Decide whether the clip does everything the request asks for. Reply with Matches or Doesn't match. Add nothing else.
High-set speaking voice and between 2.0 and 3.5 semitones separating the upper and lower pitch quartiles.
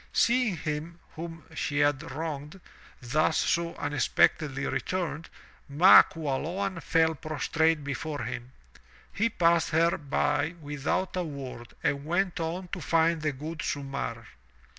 Doesn't match